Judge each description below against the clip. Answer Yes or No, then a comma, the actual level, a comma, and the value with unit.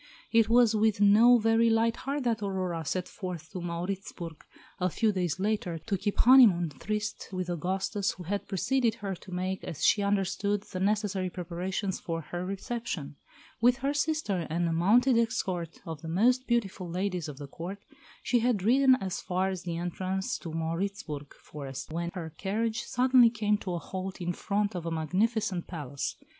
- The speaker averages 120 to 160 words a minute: No, average, 180 wpm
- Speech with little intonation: No, average, 4.2 semitones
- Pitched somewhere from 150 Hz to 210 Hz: Yes, high, 190 Hz